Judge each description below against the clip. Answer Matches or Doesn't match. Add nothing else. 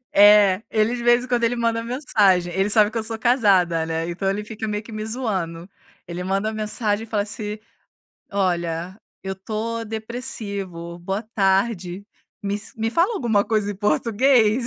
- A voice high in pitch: Matches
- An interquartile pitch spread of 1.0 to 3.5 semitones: Matches